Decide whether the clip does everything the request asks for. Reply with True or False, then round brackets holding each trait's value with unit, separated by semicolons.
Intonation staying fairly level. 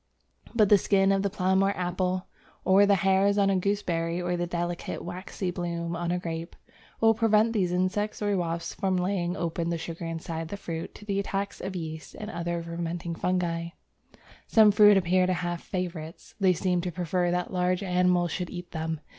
True (2.3 semitones)